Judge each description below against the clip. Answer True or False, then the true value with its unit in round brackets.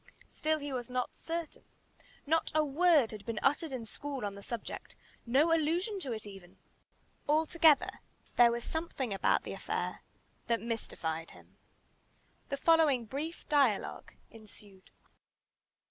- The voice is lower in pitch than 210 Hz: False (270 Hz)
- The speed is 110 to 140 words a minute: True (135 wpm)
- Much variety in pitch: True (5.8 semitones)